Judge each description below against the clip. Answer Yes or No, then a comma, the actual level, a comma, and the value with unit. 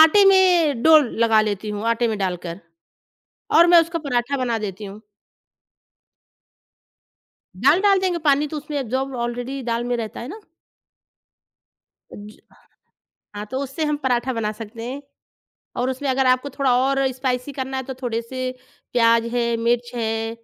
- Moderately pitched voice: No, very high, 250 Hz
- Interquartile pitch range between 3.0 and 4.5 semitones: Yes, average, 3.7 semitones